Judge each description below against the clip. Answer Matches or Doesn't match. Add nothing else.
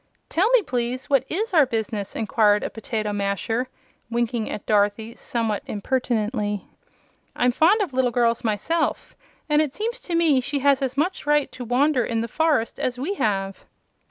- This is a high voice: Matches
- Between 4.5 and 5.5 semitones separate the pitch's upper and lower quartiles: Matches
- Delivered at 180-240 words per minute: Doesn't match